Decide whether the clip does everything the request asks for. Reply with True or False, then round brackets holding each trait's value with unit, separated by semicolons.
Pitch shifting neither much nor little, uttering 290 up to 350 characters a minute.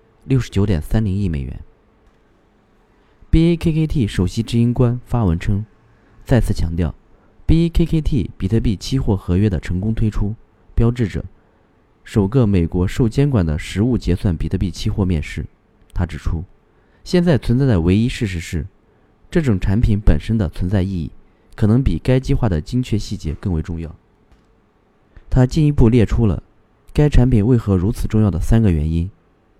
False (4.3 semitones; 255 characters per minute)